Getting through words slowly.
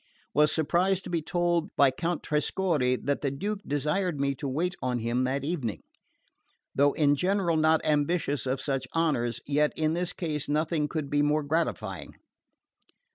No: average, 165 wpm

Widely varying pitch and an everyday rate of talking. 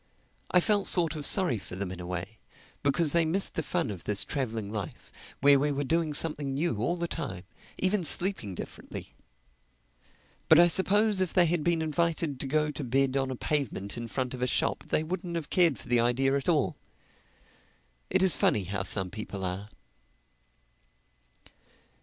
Yes: wide, 7.0 semitones; average, 180 wpm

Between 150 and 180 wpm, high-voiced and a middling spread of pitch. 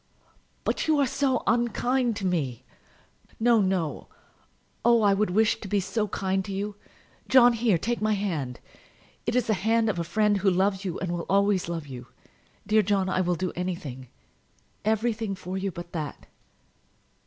Yes: average, 175 wpm; high, 200 Hz; average, 3.7 semitones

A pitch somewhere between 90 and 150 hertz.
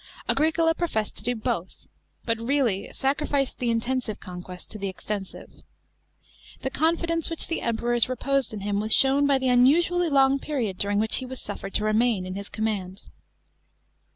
No: high, 240 Hz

